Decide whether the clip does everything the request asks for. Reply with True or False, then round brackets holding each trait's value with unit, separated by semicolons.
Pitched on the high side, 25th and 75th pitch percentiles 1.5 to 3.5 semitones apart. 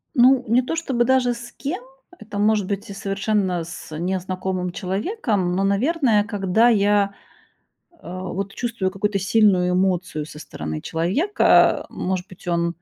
False (200 Hz; 4.2 semitones)